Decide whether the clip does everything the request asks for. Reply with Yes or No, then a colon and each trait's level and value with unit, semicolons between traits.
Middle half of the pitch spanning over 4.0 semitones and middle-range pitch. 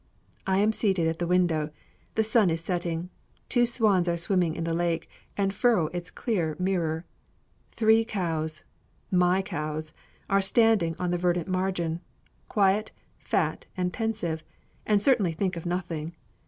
No: average, 3.3 semitones; medium, 180 Hz